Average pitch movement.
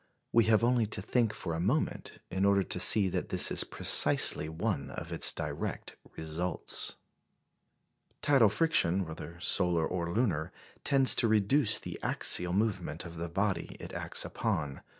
Yes: average, 4.9 semitones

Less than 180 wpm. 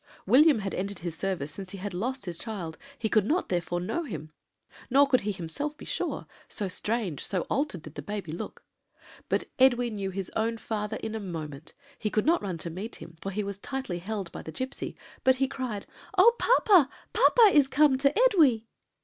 No: fast, 205 wpm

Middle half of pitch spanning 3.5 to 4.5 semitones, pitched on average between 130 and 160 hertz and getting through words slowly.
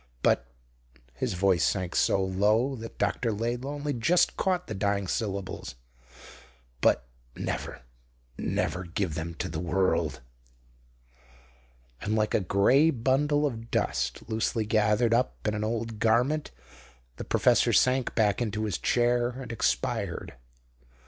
No: average, 3.9 semitones; low, 110 Hz; slow, 130 wpm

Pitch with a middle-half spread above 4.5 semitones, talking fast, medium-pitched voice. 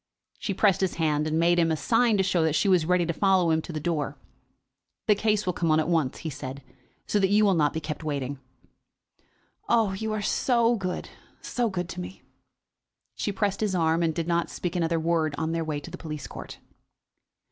No: average, 3.8 semitones; fast, 220 wpm; medium, 170 Hz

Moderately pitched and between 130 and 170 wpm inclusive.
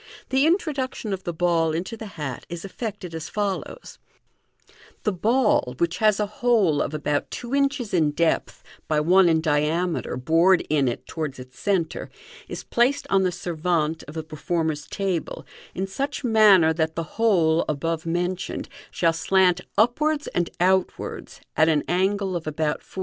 Yes: medium, 175 Hz; average, 165 wpm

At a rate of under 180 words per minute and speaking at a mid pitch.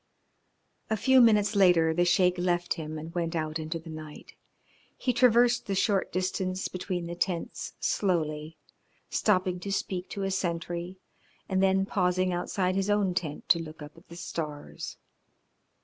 Yes: average, 160 wpm; medium, 180 Hz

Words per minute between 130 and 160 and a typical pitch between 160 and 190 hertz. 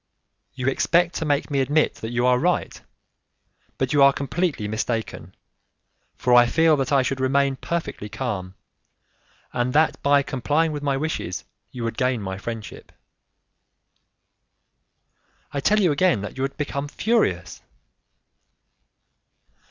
No: slow, 135 wpm; low, 135 Hz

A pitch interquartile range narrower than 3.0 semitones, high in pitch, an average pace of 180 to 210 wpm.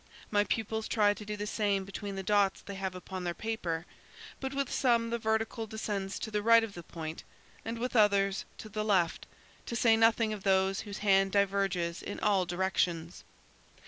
Yes: narrow, 2.4 semitones; high, 205 Hz; average, 190 wpm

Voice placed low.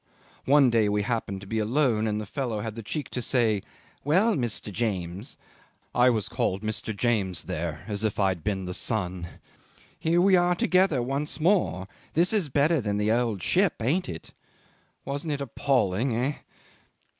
Yes: low, 115 Hz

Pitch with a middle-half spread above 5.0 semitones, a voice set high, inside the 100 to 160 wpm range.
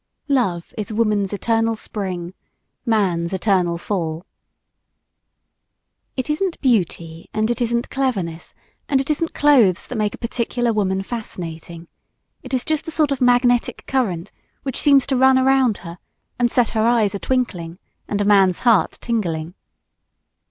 Yes: wide, 5.6 semitones; high, 220 Hz; average, 145 wpm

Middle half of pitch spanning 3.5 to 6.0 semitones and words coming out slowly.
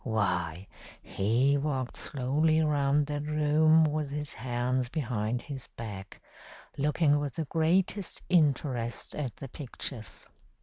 Yes: average, 3.9 semitones; slow, 120 wpm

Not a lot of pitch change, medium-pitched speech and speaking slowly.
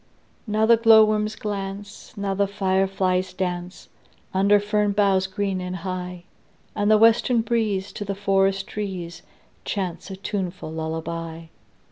No: narrow, 2.1 semitones; high, 195 Hz; slow, 130 wpm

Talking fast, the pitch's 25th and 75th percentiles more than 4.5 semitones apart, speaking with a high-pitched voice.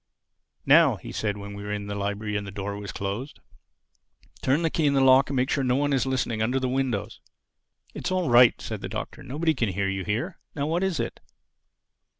No: fast, 220 wpm; wide, 5.5 semitones; low, 125 Hz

